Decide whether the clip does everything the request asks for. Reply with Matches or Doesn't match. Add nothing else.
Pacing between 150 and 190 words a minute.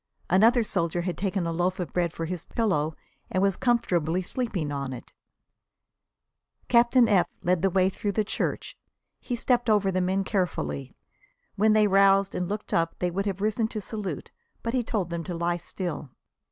Matches